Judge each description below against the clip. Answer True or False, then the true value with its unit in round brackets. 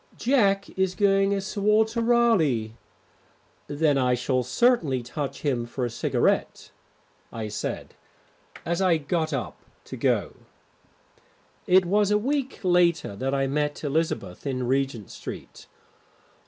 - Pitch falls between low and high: True (160 Hz)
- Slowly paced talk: True (130 wpm)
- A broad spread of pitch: True (7.3 semitones)